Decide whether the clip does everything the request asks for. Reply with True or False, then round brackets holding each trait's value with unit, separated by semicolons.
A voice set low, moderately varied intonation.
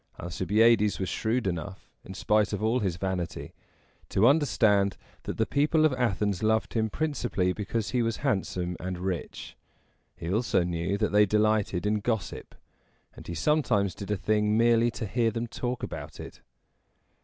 True (105 Hz; 3.6 semitones)